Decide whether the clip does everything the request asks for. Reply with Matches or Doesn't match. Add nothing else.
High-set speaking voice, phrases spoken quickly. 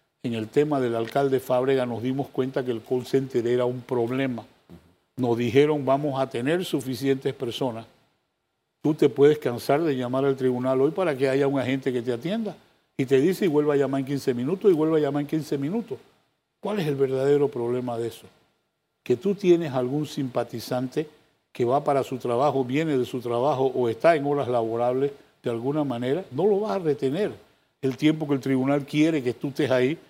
Doesn't match